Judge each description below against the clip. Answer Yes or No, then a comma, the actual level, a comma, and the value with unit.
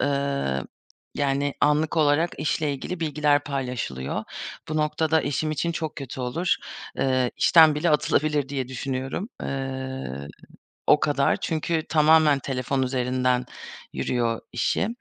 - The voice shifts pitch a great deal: No, average, 3.0 semitones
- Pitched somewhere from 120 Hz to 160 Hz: Yes, medium, 140 Hz